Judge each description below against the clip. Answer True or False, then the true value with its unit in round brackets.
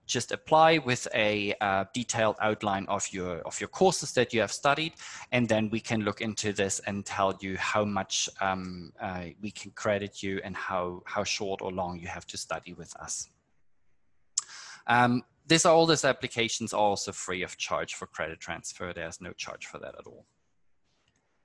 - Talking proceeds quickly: True (185 wpm)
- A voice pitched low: True (105 Hz)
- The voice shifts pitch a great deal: False (4.1 semitones)